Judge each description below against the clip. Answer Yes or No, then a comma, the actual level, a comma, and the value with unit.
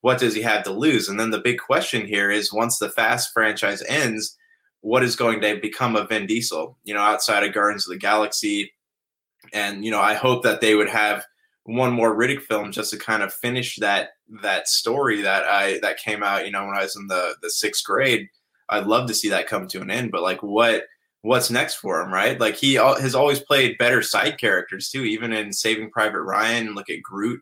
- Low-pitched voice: Yes, low, 110 Hz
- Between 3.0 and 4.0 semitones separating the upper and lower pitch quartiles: Yes, average, 3.4 semitones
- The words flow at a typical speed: No, fast, 230 wpm